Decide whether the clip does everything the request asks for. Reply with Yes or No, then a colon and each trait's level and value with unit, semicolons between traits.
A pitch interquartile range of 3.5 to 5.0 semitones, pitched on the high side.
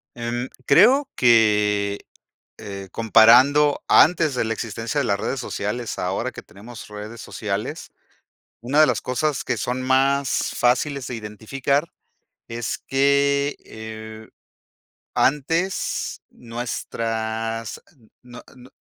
No: average, 4.0 semitones; low, 120 Hz